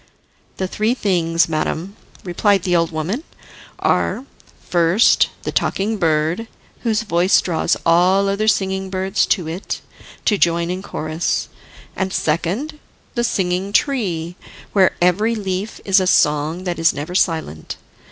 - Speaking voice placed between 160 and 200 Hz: Yes, medium, 185 Hz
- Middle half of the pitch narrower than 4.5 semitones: Yes, average, 3.3 semitones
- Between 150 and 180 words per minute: No, slow, 135 wpm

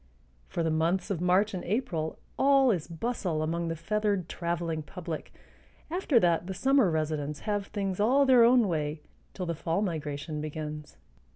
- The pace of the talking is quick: No, average, 165 wpm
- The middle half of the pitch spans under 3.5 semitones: No, average, 5.0 semitones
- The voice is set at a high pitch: No, medium, 175 Hz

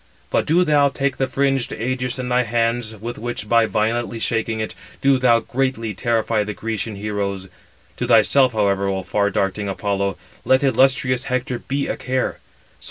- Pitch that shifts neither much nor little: Yes, average, 3.6 semitones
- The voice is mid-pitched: No, low, 115 Hz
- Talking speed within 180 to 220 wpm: No, average, 165 wpm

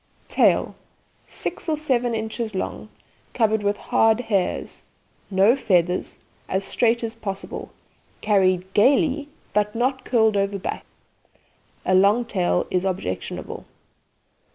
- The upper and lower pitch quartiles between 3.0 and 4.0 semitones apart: Yes, average, 3.7 semitones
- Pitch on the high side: Yes, high, 210 Hz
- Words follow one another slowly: Yes, slow, 115 wpm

